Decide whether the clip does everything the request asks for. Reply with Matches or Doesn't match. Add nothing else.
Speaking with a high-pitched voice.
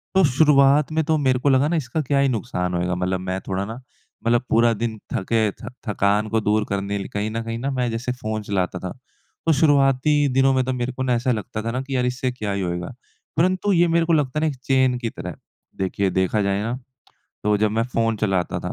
Doesn't match